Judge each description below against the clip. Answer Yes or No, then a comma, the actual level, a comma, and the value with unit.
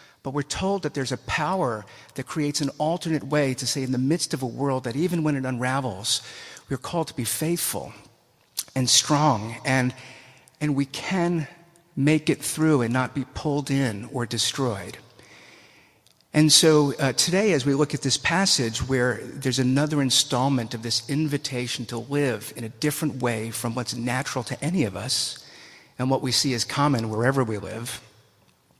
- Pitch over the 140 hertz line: No, low, 135 Hz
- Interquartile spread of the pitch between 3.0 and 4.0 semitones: Yes, average, 3.3 semitones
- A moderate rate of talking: Yes, average, 180 wpm